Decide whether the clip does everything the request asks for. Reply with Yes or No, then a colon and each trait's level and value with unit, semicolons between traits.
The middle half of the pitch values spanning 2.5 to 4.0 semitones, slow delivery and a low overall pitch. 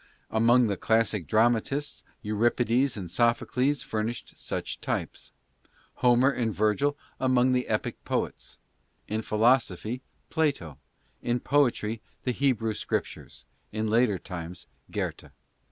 Yes: average, 2.9 semitones; slow, 110 wpm; low, 115 Hz